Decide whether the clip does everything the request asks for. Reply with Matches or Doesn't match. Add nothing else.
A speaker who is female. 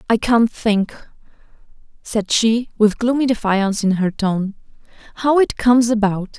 Matches